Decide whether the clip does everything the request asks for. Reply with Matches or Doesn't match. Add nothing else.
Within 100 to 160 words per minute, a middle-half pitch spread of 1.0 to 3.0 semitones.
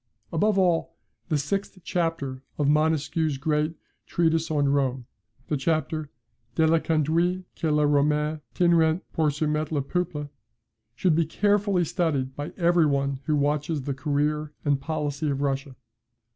Matches